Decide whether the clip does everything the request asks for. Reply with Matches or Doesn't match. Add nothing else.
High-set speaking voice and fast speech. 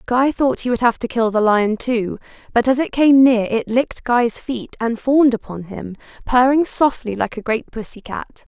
Matches